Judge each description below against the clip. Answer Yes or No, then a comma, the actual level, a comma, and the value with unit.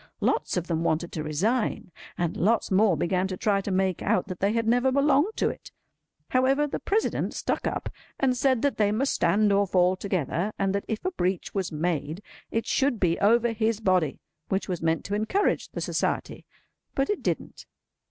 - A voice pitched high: Yes, high, 200 Hz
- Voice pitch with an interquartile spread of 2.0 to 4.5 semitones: No, average, 4.9 semitones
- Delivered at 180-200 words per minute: Yes, average, 190 wpm